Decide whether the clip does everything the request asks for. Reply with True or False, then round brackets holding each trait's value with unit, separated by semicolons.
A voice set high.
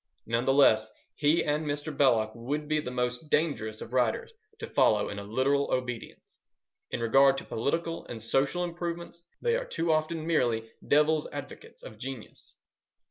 False (140 Hz)